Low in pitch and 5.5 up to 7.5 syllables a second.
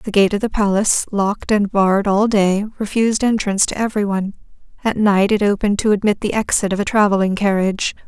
No: high, 205 Hz; 6.3 syllables/s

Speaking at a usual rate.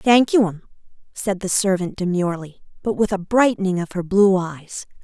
Yes: average, 180 wpm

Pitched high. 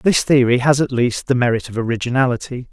No: low, 125 Hz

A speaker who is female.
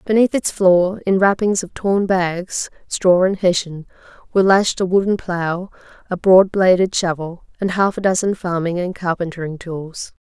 Yes: female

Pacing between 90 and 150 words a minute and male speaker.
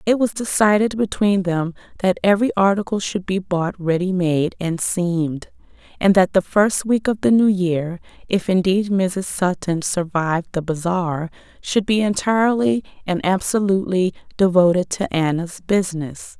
No: average, 145 wpm; female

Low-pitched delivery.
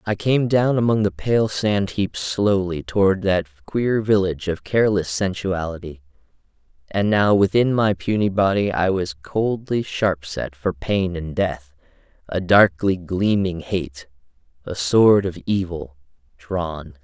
Yes: very low, 95 Hz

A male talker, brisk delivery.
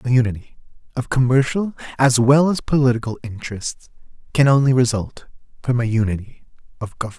No: male; average, 140 wpm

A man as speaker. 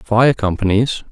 Yes: male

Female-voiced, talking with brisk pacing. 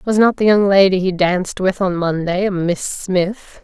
Yes: female; fast, 215 wpm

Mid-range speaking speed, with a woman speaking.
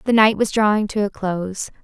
No: fast, 230 wpm; female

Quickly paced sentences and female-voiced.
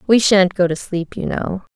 Yes: fast, 240 wpm; female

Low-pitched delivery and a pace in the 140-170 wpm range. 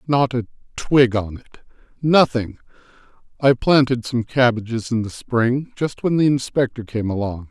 Yes: low, 125 Hz; average, 145 wpm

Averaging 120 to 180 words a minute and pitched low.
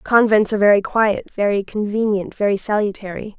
No: average, 140 wpm; high, 205 Hz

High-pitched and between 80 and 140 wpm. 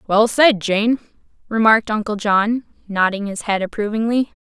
Yes: high, 215 Hz; slow, 135 wpm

